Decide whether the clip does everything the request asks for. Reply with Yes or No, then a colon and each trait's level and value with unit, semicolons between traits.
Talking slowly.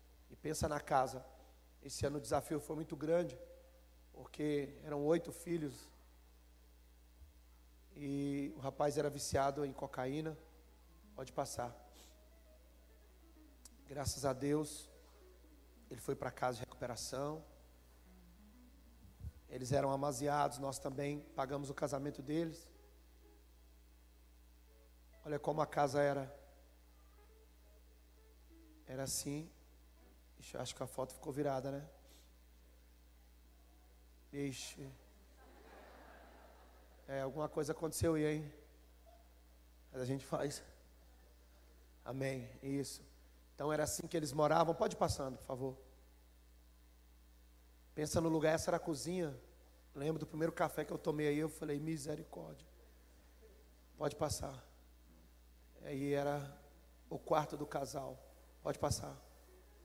Yes: slow, 110 wpm